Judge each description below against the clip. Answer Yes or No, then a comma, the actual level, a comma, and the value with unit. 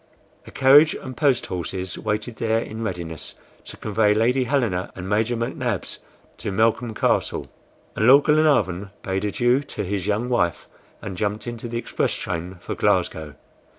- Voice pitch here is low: Yes, low, 110 Hz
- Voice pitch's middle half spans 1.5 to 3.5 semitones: No, average, 4.3 semitones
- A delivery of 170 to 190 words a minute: No, average, 155 wpm